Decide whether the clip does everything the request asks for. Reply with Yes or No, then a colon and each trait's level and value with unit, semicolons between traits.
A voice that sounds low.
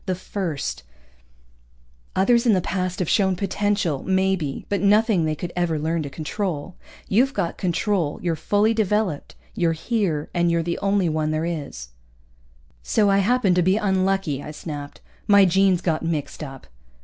No: medium, 180 Hz